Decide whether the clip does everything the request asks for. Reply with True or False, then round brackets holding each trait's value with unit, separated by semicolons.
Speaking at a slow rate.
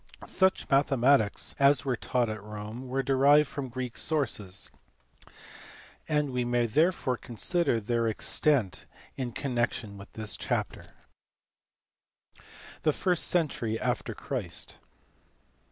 True (115 wpm)